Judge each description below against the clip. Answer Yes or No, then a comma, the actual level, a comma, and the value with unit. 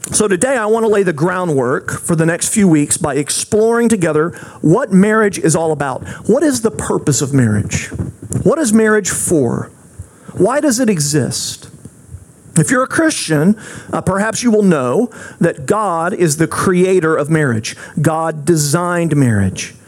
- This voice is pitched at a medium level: Yes, medium, 170 Hz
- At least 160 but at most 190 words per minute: Yes, average, 165 wpm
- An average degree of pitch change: No, wide, 6.1 semitones